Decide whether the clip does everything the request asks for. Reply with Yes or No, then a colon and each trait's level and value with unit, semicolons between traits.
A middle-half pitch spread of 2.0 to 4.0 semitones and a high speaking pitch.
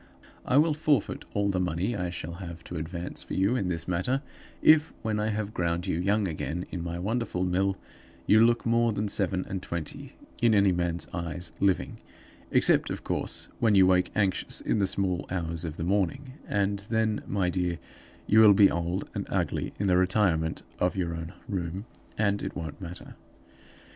No: average, 3.3 semitones; very low, 95 Hz